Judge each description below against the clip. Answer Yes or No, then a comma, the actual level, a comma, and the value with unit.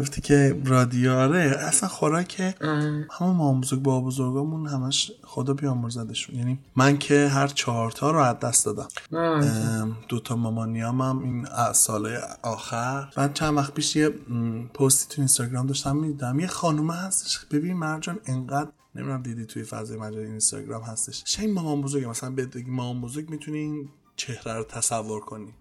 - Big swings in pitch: No, average, 3.7 semitones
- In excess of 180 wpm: No, average, 150 wpm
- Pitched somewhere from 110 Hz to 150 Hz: Yes, low, 135 Hz